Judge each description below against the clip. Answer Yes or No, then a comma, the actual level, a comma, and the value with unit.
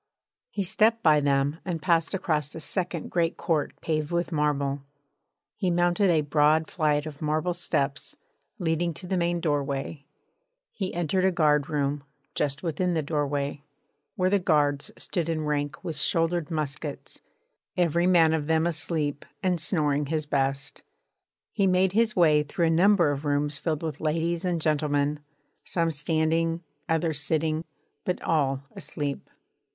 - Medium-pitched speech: Yes, medium, 160 Hz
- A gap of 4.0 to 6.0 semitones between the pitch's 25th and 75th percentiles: No, average, 2.8 semitones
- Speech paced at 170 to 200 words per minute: No, average, 150 wpm